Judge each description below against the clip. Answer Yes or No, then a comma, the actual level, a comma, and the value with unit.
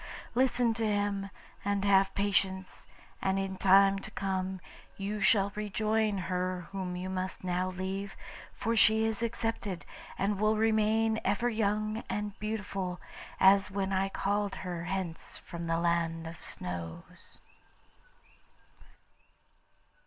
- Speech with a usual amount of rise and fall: No, narrow, 2.3 semitones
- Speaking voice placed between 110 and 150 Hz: No, high, 195 Hz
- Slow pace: Yes, slow, 125 wpm